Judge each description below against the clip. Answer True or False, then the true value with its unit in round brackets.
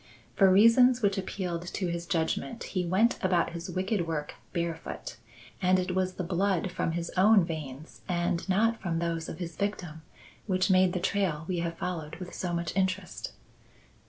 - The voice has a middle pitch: True (180 Hz)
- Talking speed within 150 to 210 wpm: True (175 wpm)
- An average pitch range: False (2.2 semitones)